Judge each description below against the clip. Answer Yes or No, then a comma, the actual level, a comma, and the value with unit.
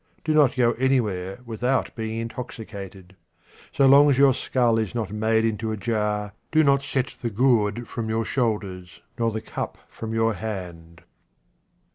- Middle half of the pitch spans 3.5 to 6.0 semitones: No, average, 3.1 semitones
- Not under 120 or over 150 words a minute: No, average, 160 wpm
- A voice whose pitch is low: Yes, low, 115 Hz